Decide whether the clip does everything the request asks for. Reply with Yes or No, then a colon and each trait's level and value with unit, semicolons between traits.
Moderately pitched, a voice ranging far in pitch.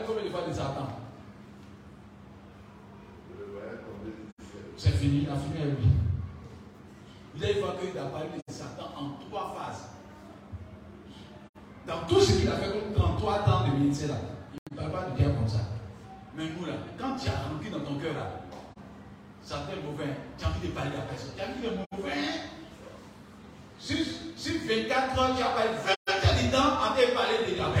No: low, 120 Hz; wide, 8.6 semitones